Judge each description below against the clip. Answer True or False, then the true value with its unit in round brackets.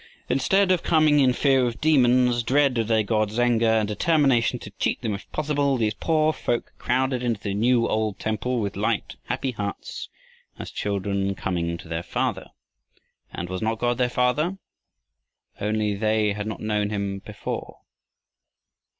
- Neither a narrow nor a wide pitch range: True (3.9 semitones)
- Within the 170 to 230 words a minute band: False (160 wpm)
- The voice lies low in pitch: True (115 Hz)